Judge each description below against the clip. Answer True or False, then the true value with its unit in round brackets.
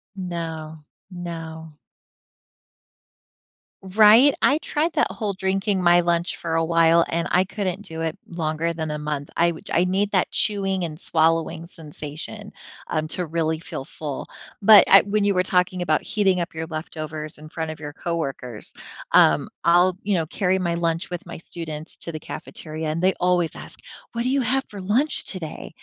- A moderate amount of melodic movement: True (3.0 semitones)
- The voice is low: False (170 Hz)